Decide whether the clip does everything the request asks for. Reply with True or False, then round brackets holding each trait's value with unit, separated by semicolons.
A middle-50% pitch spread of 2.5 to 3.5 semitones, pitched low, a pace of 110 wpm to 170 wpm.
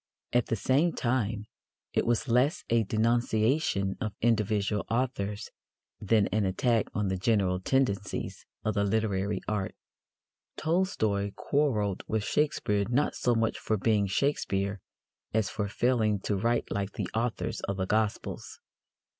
True (2.9 semitones; 110 Hz; 140 wpm)